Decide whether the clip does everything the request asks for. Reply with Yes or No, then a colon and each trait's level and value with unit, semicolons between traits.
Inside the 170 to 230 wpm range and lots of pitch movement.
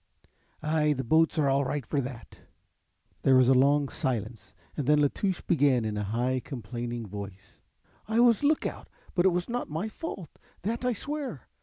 Yes: average, 180 wpm; wide, 6.6 semitones